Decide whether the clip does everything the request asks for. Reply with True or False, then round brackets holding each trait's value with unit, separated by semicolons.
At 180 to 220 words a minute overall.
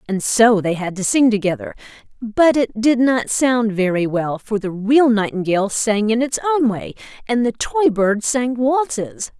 True (185 wpm)